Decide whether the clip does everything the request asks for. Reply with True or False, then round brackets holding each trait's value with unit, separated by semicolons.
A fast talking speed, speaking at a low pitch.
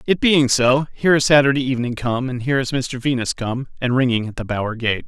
True (235 wpm; 130 Hz)